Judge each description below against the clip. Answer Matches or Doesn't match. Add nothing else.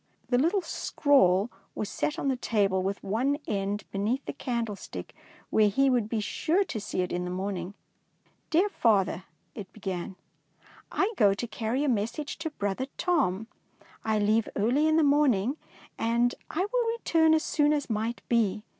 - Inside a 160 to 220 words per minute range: Matches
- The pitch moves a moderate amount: Doesn't match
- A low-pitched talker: Doesn't match